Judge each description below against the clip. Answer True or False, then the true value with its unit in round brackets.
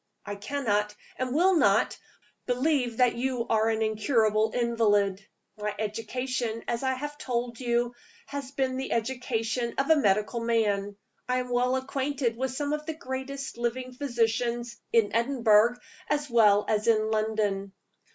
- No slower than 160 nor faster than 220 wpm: False (150 wpm)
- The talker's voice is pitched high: True (235 Hz)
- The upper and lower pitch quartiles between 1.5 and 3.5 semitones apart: True (3.1 semitones)